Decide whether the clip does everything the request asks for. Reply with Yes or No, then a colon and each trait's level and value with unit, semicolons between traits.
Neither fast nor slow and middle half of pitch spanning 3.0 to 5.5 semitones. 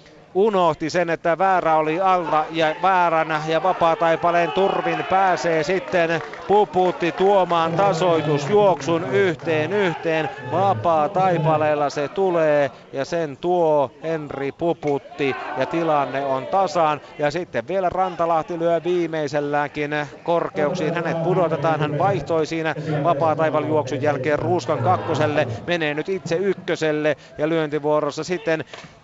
No: average, 110 wpm; narrow, 2.5 semitones